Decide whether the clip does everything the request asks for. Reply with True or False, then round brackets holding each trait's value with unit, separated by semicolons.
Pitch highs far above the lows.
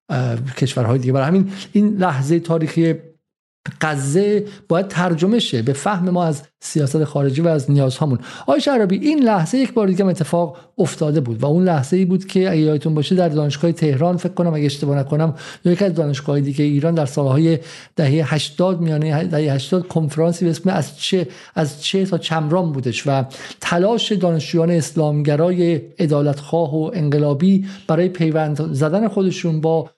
False (3.3 semitones)